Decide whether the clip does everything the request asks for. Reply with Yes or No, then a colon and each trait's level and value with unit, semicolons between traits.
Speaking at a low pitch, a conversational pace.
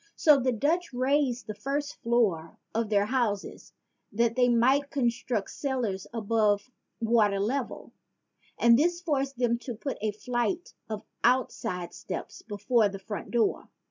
No: high, 235 Hz; average, 145 wpm